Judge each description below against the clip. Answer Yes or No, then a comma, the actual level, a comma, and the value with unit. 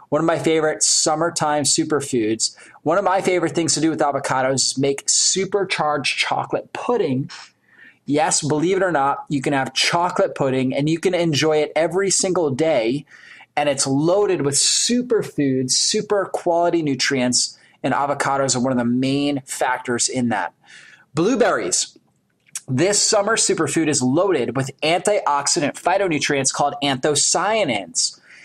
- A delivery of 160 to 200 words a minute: No, average, 140 wpm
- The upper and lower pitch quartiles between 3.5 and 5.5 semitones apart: Yes, average, 3.9 semitones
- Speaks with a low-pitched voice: No, medium, 150 Hz